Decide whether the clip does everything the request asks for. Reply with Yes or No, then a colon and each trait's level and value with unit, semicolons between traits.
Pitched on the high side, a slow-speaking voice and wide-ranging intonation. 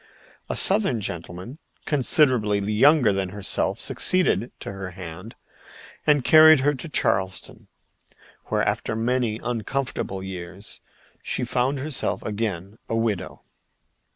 No: low, 110 Hz; slow, 115 wpm; wide, 5.7 semitones